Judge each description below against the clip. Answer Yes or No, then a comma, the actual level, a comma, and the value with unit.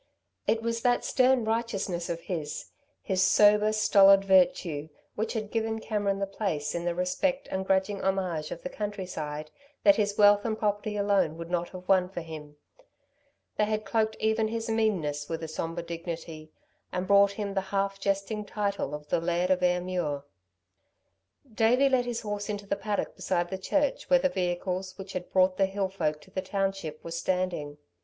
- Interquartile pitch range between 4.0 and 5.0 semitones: No, average, 3.4 semitones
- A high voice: Yes, high, 195 Hz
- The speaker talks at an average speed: Yes, average, 180 wpm